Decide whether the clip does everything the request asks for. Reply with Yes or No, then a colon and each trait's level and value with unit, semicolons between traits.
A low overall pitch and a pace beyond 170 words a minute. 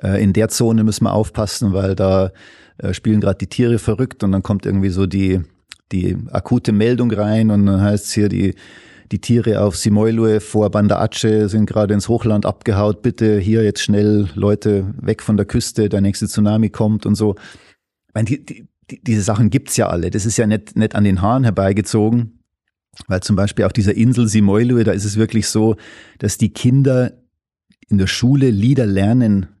Yes: low, 105 Hz; fast, 190 wpm